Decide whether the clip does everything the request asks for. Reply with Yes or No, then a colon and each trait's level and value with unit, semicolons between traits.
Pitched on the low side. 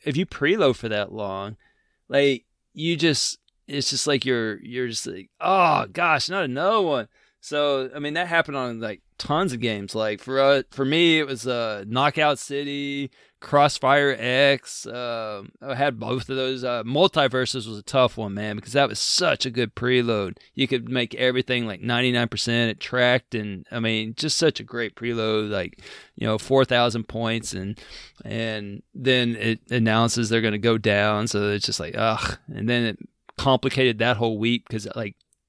Yes: low, 120 Hz